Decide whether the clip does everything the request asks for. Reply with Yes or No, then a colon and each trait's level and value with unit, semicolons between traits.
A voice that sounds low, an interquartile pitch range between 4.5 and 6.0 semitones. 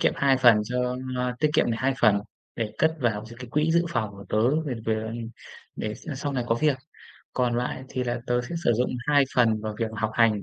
No: low, 120 Hz; average, 3.2 semitones